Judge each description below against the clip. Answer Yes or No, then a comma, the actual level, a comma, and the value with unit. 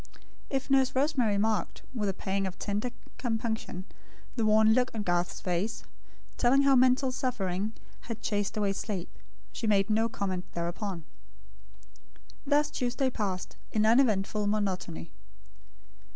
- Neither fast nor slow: No, slow, 130 wpm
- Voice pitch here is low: No, high, 215 Hz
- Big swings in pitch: No, average, 4.2 semitones